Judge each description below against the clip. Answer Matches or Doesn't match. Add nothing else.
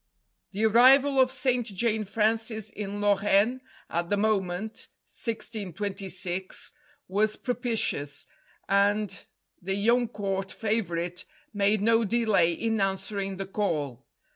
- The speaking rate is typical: Doesn't match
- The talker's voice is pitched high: Matches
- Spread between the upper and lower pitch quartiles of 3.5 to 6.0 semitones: Doesn't match